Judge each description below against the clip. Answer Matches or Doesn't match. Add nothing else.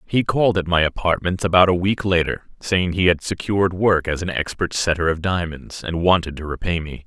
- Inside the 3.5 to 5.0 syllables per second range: Doesn't match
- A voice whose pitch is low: Matches